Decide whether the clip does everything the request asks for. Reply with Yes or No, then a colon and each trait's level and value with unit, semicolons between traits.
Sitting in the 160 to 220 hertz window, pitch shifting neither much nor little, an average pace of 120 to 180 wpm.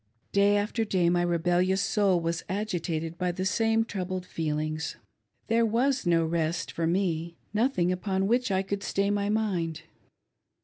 Yes: medium, 185 Hz; average, 3.4 semitones; average, 160 wpm